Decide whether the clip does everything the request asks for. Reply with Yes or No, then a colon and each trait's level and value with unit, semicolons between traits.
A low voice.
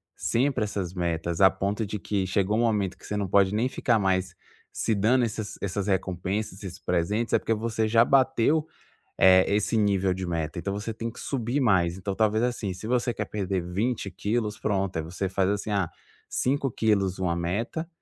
Yes: low, 100 Hz